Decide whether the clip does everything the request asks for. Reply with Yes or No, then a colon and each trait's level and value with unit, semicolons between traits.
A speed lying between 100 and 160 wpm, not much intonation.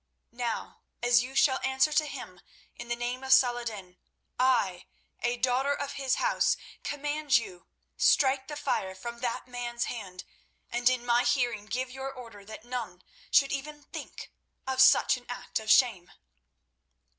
Yes: average, 155 wpm; narrow, 2.2 semitones